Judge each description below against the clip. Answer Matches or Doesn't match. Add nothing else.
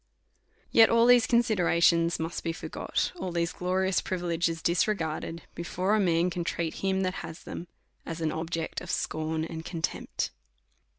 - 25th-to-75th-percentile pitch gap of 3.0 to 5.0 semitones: Doesn't match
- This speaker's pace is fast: Doesn't match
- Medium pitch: Matches